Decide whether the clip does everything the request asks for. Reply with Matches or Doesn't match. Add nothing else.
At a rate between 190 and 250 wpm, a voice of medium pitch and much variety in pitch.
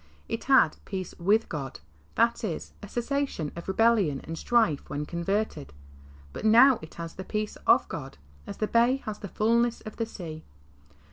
Doesn't match